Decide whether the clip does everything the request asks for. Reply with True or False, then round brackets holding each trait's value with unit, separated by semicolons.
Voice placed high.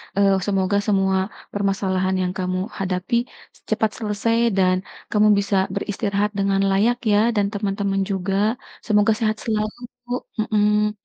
True (200 Hz)